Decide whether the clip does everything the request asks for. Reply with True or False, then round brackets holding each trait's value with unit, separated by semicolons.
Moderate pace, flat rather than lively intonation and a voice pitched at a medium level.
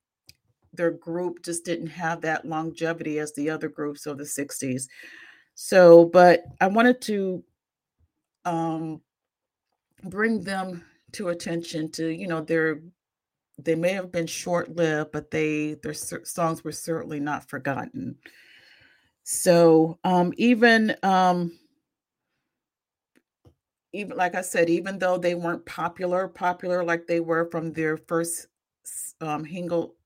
False (130 wpm; 2.1 semitones; 170 Hz)